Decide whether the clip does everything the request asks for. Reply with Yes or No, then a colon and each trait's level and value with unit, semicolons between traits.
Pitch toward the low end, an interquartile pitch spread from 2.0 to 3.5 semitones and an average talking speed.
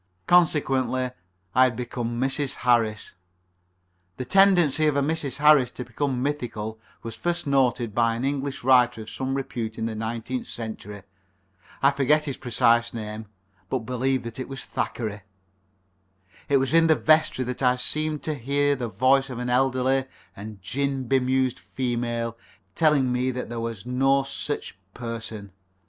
Yes: low, 130 Hz; average, 2.8 semitones; average, 155 wpm